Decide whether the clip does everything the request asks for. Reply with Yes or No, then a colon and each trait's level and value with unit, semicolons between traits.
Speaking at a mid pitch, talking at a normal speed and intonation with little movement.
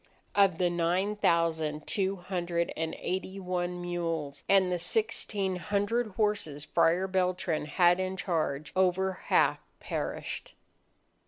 No: medium, 180 Hz; slow, 120 wpm; narrow, 2.2 semitones